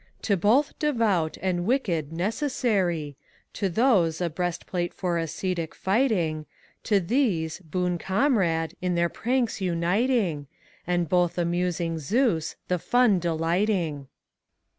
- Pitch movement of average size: Yes, average, 4.5 semitones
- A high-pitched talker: No, medium, 180 Hz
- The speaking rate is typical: No, slow, 130 wpm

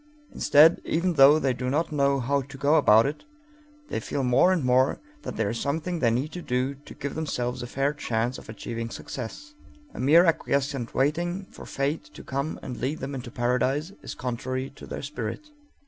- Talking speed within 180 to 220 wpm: Yes, average, 195 wpm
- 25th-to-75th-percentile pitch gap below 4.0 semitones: Yes, average, 3.5 semitones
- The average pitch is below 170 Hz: Yes, medium, 140 Hz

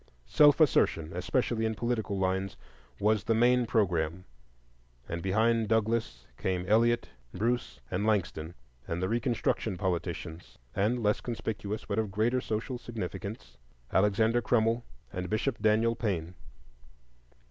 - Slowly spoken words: Yes, slow, 125 wpm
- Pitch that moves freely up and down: No, average, 3.8 semitones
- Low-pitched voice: Yes, low, 110 Hz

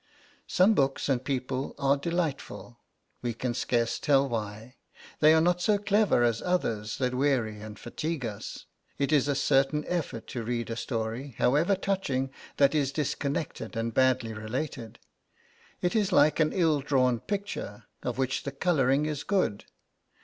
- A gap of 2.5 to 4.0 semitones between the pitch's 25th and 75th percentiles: No, average, 4.6 semitones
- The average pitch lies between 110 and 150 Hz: Yes, low, 135 Hz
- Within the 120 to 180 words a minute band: Yes, average, 155 wpm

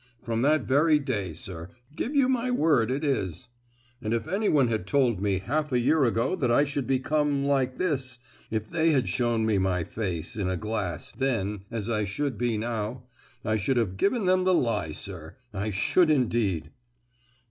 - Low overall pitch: Yes, low, 120 Hz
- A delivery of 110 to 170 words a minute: No, average, 180 wpm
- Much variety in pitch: Yes, wide, 5.7 semitones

